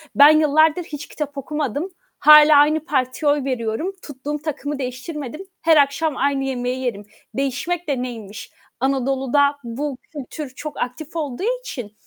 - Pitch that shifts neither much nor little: Yes, average, 3.0 semitones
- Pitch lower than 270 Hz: No, very high, 285 Hz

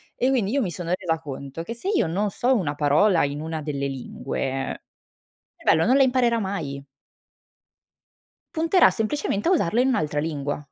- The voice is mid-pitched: Yes, medium, 170 Hz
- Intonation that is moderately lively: No, wide, 8.4 semitones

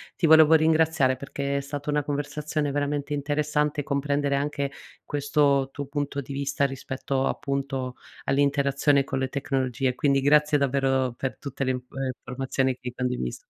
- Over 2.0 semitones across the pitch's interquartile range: No, narrow, 1.5 semitones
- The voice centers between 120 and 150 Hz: Yes, medium, 140 Hz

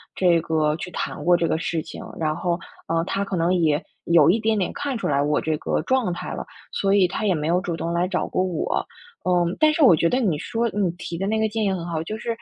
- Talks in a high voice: No, medium, 180 Hz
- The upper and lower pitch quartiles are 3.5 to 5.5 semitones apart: Yes, average, 3.8 semitones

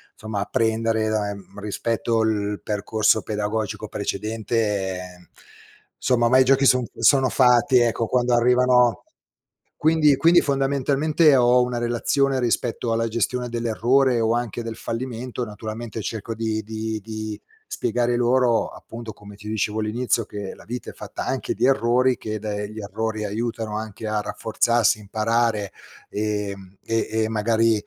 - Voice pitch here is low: Yes, low, 115 Hz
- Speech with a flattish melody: Yes, narrow, 2.3 semitones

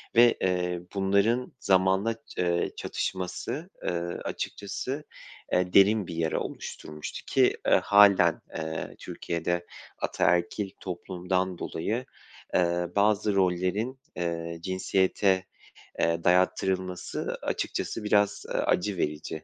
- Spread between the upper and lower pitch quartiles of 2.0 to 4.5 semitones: Yes, narrow, 2.6 semitones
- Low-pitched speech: Yes, very low, 95 Hz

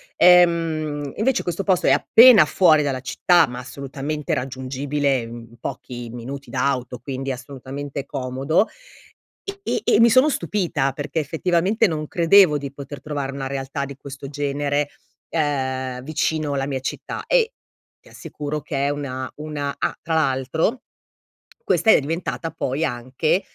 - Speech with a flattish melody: No, average, 3.3 semitones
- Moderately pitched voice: Yes, medium, 145 Hz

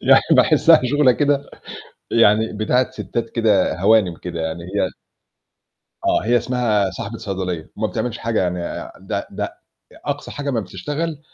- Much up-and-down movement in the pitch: No, average, 4.7 semitones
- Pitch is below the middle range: Yes, low, 110 Hz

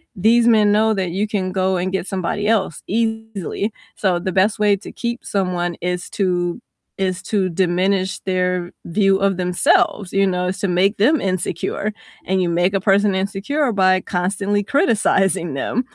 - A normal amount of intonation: No, narrow, 2.3 semitones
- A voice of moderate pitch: No, high, 195 Hz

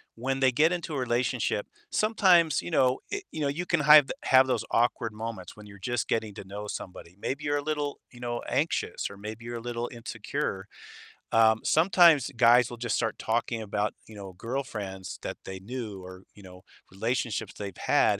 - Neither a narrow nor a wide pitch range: Yes, average, 4.4 semitones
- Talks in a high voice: No, low, 120 Hz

